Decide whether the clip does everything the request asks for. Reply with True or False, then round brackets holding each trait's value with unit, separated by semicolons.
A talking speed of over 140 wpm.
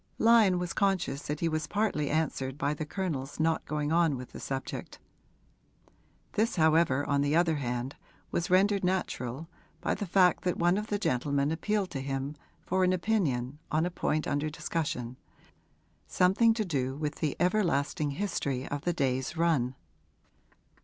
True (160 wpm)